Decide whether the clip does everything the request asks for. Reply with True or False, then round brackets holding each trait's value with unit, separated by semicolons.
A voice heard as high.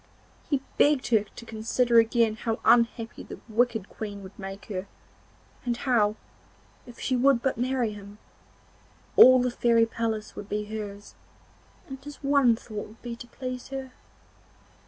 True (230 Hz)